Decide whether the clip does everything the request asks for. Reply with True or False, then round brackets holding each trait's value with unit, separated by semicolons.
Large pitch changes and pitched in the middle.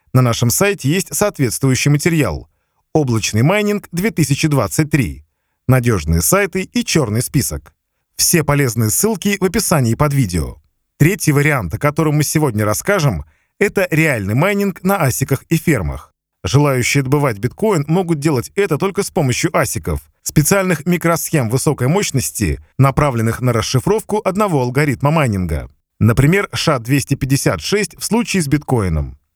True (6.8 semitones; 145 Hz)